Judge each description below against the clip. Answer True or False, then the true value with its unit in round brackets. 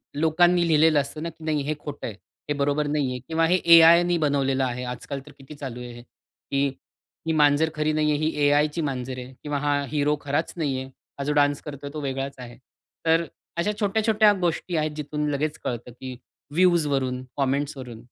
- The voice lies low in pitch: False (145 Hz)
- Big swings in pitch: False (2.8 semitones)